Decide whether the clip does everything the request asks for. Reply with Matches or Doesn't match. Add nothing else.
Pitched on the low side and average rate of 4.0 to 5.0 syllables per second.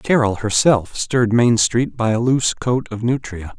Matches